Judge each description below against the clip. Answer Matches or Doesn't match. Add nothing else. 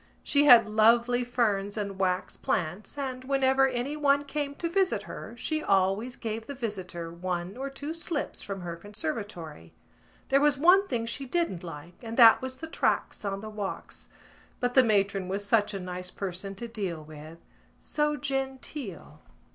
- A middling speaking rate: Matches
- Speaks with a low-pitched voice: Doesn't match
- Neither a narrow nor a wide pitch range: Doesn't match